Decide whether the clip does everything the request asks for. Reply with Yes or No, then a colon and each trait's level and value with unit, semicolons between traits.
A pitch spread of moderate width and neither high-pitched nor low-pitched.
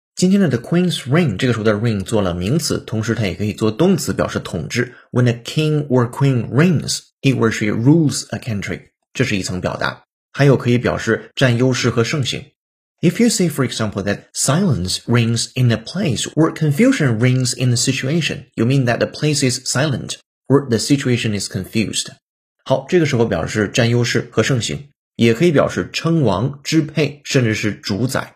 No: average, 4.8 semitones; low, 125 Hz